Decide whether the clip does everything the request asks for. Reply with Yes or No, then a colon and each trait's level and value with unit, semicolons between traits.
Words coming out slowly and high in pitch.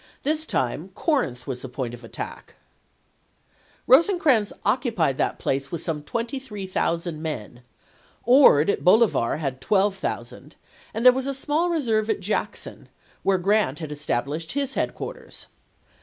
Yes: slow, 130 wpm; high, 195 Hz